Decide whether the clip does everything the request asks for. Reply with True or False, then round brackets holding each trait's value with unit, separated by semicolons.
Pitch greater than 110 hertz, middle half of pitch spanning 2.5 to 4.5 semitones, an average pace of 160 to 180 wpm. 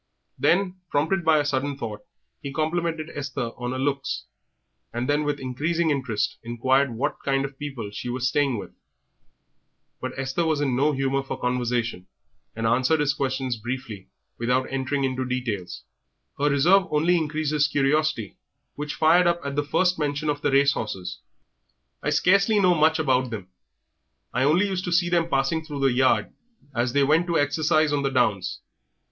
True (140 Hz; 3.4 semitones; 175 wpm)